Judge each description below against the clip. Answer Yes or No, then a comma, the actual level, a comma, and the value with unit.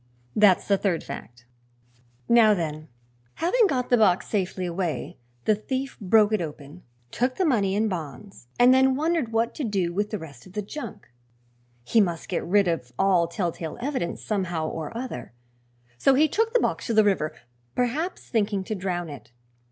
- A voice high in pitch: Yes, high, 205 Hz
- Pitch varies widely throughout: Yes, wide, 5.9 semitones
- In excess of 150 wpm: Yes, average, 175 wpm